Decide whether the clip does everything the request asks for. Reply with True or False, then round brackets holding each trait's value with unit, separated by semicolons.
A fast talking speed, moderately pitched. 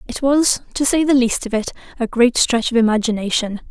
False (210 wpm; 245 Hz)